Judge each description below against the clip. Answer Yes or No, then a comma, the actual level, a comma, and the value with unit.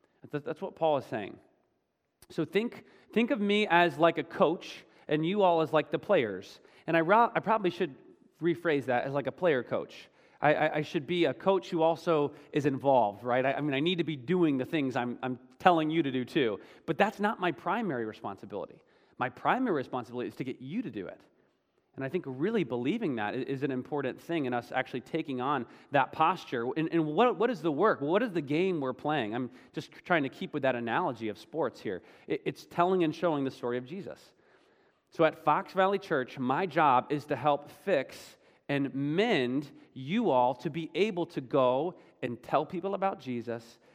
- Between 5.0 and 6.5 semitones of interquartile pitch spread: Yes, average, 5.3 semitones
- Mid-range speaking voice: Yes, medium, 155 Hz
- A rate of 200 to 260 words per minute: Yes, fast, 205 wpm